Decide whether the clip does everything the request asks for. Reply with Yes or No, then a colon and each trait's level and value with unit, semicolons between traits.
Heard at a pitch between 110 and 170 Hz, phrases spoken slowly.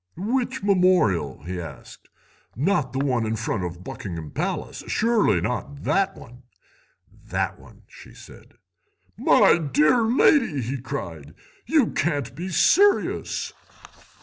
Yes: medium, 140 Hz; slow, 120 wpm